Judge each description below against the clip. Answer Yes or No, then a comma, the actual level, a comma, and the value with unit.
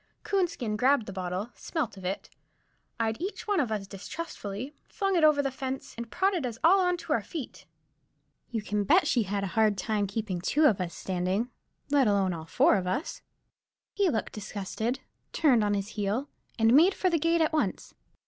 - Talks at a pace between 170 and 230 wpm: Yes, average, 195 wpm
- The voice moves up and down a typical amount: No, wide, 7.5 semitones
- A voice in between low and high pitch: No, high, 230 Hz